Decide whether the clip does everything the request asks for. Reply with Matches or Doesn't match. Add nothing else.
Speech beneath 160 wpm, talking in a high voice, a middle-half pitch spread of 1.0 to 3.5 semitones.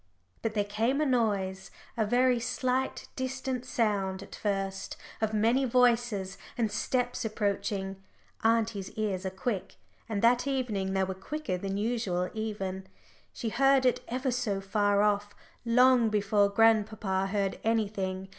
Doesn't match